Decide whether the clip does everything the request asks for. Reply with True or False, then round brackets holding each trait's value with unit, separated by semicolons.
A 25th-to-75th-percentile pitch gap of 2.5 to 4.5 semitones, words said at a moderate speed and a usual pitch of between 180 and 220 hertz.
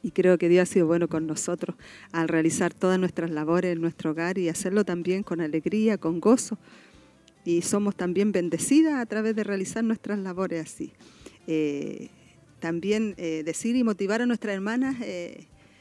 True (4.1 semitones; 170 wpm; 185 Hz)